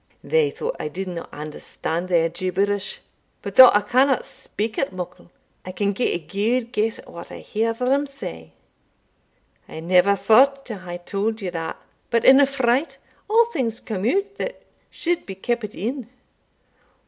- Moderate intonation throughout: No, wide, 6.0 semitones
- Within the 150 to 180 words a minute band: Yes, average, 165 wpm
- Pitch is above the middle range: Yes, high, 215 Hz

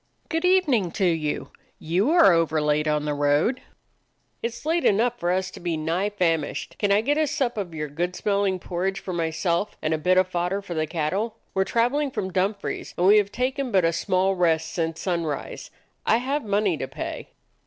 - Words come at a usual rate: No, fast, 210 wpm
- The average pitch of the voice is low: No, medium, 185 Hz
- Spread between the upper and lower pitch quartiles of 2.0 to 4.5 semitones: No, average, 5.0 semitones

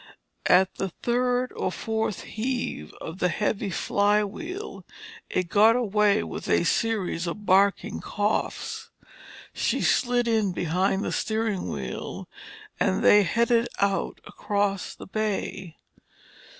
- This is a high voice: Yes, high, 210 Hz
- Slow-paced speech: Yes, slow, 120 wpm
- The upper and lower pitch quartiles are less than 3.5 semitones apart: Yes, average, 3.1 semitones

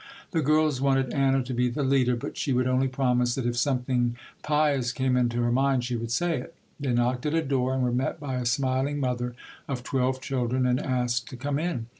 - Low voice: Yes, low, 130 Hz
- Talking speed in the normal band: No, fast, 225 wpm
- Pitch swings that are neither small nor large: No, narrow, 1.9 semitones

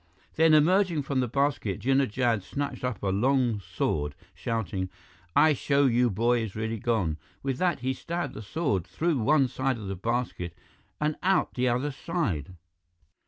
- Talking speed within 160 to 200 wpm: Yes, average, 165 wpm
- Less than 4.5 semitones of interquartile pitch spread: No, wide, 5.4 semitones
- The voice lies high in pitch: No, low, 125 Hz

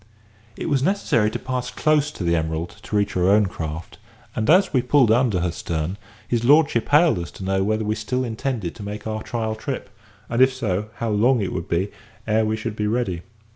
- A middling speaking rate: No, fast, 215 wpm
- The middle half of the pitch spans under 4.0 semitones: No, average, 4.8 semitones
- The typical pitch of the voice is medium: No, low, 110 Hz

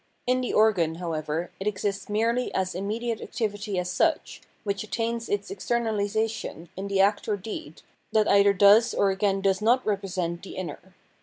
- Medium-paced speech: Yes, average, 165 wpm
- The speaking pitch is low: No, high, 200 Hz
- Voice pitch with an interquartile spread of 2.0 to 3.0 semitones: Yes, narrow, 2.6 semitones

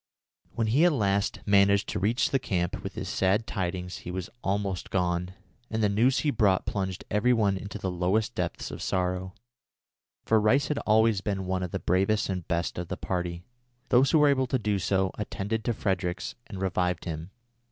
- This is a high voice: No, low, 100 Hz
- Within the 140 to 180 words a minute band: No, average, 195 wpm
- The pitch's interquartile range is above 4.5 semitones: No, average, 3.2 semitones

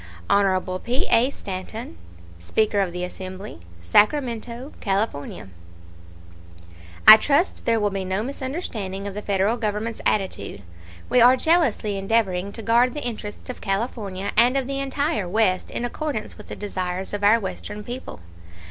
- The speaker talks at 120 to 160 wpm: Yes, average, 150 wpm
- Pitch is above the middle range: Yes, high, 210 Hz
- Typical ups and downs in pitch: Yes, average, 4.0 semitones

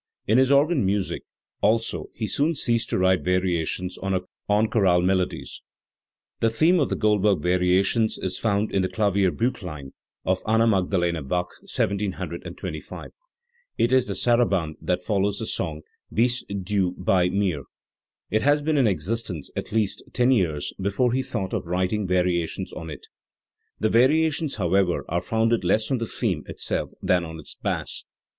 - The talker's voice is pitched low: Yes, low, 100 Hz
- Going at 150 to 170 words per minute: Yes, average, 155 wpm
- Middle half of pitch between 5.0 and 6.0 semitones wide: No, average, 4.1 semitones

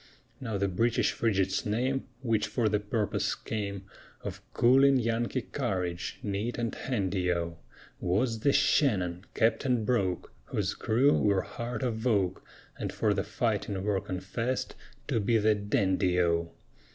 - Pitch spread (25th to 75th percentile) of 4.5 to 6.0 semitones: No, average, 3.9 semitones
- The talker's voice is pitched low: Yes, low, 105 Hz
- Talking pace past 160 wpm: No, average, 140 wpm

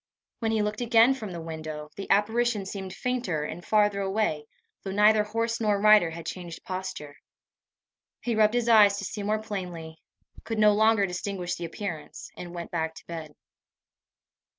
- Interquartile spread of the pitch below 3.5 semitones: No, average, 4.0 semitones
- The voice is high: Yes, high, 200 Hz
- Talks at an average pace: Yes, average, 170 wpm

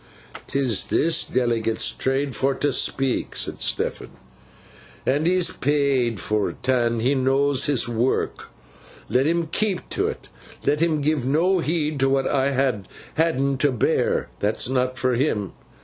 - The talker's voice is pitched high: No, low, 135 Hz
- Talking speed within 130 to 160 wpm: Yes, average, 150 wpm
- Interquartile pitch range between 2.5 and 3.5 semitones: Yes, average, 2.8 semitones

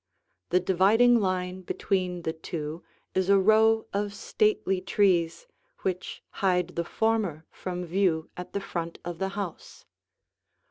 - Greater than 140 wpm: No, slow, 135 wpm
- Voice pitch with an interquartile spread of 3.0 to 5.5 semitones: No, narrow, 2.5 semitones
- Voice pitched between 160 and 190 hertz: Yes, medium, 185 Hz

